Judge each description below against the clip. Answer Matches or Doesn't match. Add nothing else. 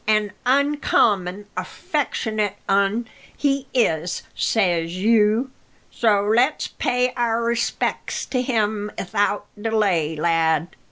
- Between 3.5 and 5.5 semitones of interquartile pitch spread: Matches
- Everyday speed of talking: Doesn't match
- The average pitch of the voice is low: Doesn't match